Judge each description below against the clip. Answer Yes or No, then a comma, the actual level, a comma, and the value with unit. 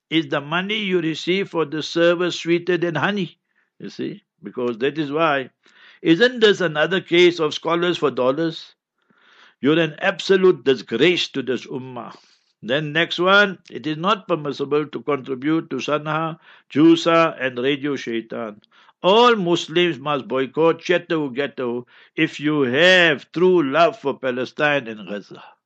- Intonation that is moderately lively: Yes, average, 3.9 semitones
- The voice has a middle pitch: Yes, medium, 160 Hz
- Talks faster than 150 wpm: No, average, 145 wpm